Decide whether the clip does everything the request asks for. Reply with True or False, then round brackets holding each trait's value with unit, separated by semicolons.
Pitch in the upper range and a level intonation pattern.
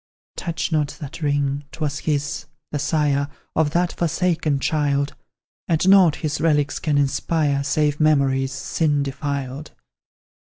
False (145 Hz; 1.9 semitones)